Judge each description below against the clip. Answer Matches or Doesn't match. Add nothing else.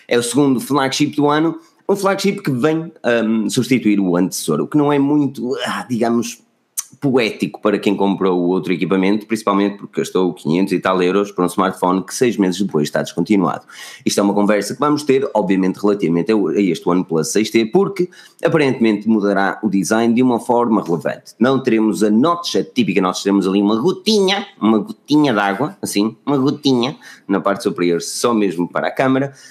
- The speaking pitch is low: Matches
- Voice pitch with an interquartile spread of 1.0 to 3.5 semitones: Doesn't match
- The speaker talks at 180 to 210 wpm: Matches